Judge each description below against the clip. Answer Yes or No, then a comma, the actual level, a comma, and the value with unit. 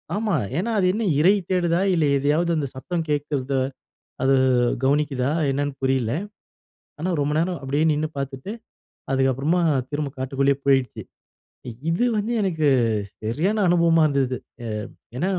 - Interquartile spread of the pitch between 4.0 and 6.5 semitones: Yes, average, 4.3 semitones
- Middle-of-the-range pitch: Yes, medium, 150 Hz